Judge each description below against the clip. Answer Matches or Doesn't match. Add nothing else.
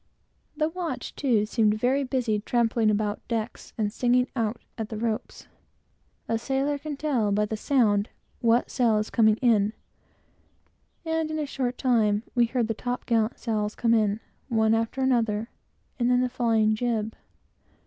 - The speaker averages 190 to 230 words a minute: Doesn't match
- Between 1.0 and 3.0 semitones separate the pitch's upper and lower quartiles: Matches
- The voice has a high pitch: Matches